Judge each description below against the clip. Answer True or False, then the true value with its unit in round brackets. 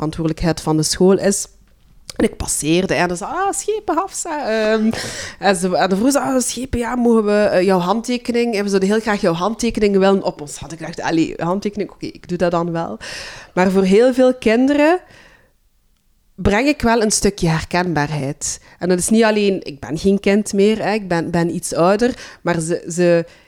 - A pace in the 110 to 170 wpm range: False (195 wpm)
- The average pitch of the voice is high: True (195 Hz)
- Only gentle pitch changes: False (4.9 semitones)